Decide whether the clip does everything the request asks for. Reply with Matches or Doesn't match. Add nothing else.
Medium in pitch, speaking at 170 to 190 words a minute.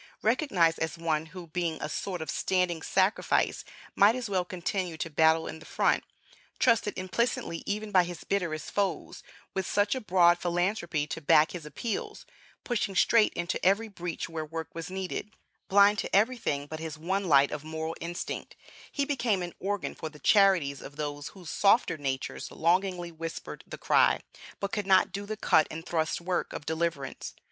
Matches